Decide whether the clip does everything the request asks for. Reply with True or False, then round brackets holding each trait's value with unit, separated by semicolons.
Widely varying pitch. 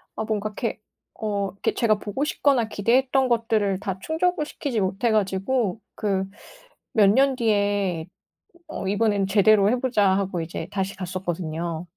False (3.2 semitones)